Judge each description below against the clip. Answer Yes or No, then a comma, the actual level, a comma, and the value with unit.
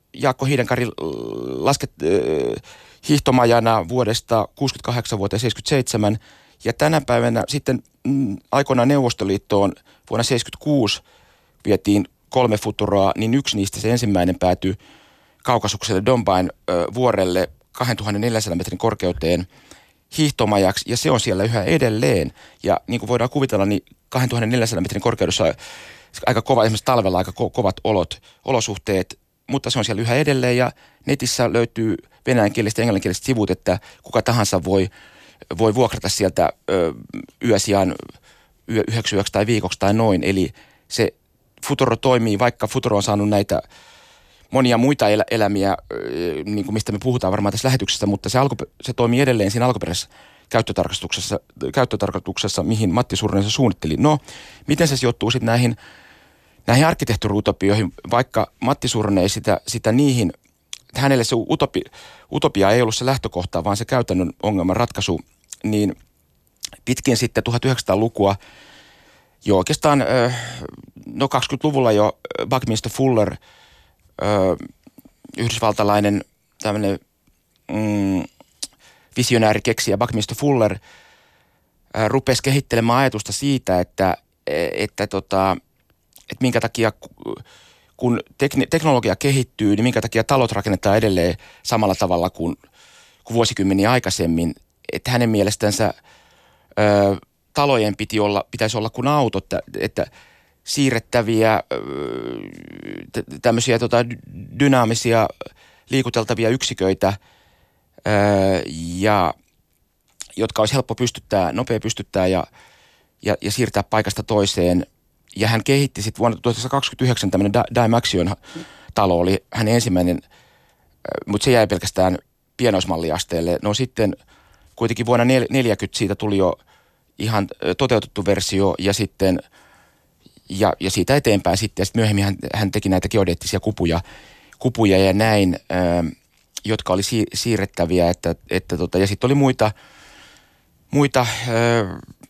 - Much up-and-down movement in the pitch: No, average, 4.0 semitones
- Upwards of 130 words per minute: No, average, 120 wpm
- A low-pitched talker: Yes, low, 110 Hz